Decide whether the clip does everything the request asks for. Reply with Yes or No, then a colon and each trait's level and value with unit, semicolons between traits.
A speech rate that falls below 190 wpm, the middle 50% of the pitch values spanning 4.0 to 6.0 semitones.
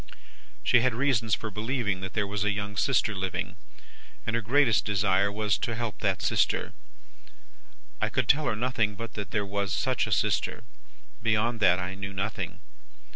No: average, 175 wpm; average, 2.7 semitones